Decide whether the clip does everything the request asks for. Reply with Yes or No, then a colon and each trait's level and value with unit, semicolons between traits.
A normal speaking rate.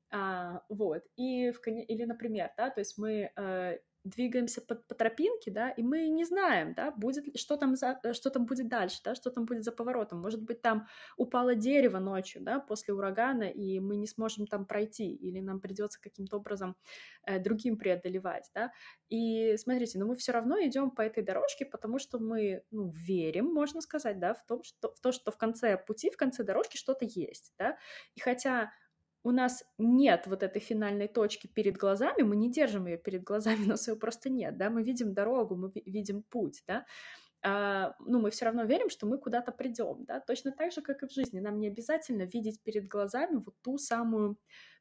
No: fast, 200 wpm